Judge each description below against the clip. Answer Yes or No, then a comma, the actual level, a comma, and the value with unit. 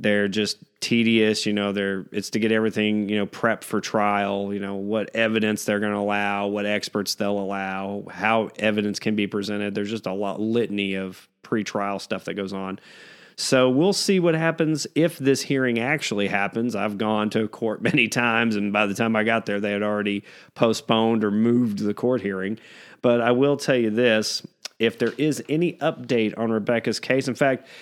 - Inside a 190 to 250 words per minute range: Yes, average, 195 wpm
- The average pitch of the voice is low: Yes, low, 110 Hz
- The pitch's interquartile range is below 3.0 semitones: Yes, narrow, 2.5 semitones